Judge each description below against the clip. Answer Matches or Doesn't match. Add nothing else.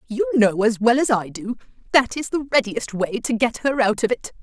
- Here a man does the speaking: Doesn't match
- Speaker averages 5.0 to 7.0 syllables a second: Matches